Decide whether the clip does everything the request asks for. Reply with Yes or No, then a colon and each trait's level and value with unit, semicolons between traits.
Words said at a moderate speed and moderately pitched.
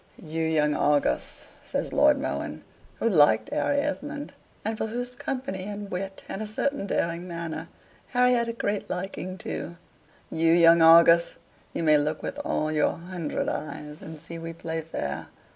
Yes: average, 165 wpm; medium, 170 Hz